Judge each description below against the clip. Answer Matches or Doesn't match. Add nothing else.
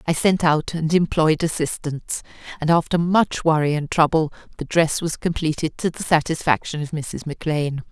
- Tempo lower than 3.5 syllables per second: Doesn't match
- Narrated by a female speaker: Matches